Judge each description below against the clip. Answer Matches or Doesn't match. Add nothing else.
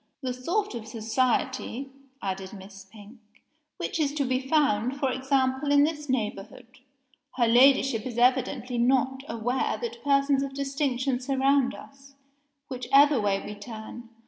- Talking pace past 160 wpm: Doesn't match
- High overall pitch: Matches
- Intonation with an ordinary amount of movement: Matches